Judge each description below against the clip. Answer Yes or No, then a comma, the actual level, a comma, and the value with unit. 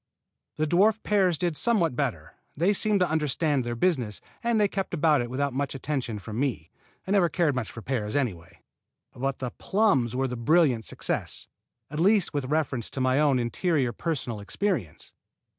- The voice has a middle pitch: Yes, medium, 145 Hz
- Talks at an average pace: Yes, average, 175 wpm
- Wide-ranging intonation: Yes, wide, 6.1 semitones